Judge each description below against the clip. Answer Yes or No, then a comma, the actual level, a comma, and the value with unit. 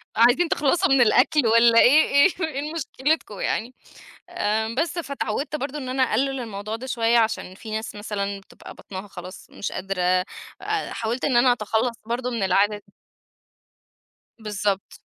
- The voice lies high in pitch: Yes, high, 230 Hz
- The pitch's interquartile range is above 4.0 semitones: Yes, average, 4.6 semitones